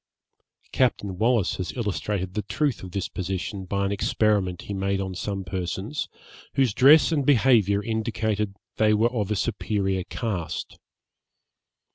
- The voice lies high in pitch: No, low, 105 Hz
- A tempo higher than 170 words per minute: No, average, 145 wpm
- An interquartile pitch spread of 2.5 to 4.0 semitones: Yes, average, 3.0 semitones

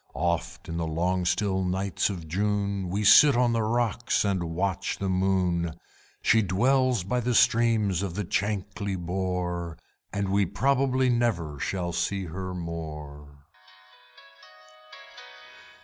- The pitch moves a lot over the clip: No, average, 3.4 semitones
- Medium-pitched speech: No, very low, 95 Hz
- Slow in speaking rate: Yes, slow, 130 wpm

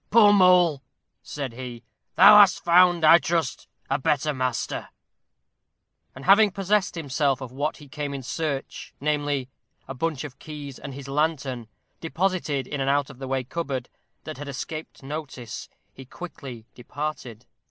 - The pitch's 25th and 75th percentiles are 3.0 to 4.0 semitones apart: Yes, average, 3.7 semitones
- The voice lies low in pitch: No, medium, 145 Hz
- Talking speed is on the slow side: No, average, 155 wpm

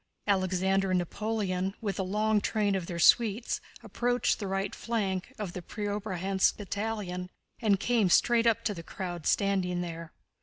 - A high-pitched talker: Yes, high, 195 Hz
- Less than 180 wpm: Yes, average, 155 wpm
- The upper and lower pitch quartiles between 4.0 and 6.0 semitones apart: No, average, 2.7 semitones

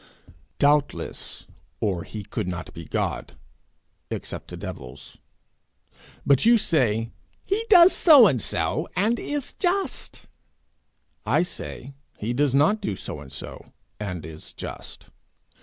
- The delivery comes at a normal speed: No, slow, 125 wpm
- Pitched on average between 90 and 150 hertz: Yes, low, 135 Hz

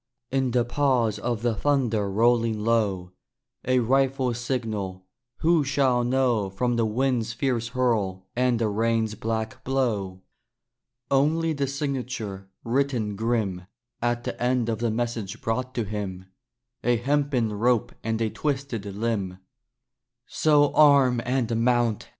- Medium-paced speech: No, slow, 130 wpm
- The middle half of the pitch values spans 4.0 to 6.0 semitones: No, average, 3.1 semitones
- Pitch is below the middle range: Yes, low, 120 Hz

